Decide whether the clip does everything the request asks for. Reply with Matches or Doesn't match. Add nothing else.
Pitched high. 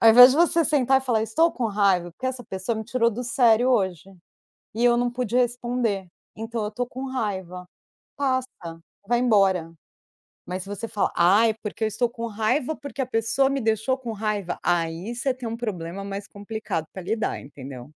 Matches